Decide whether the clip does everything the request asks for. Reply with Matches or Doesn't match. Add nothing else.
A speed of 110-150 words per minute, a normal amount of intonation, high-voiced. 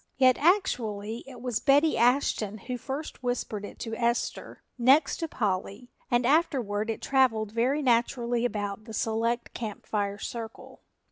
Matches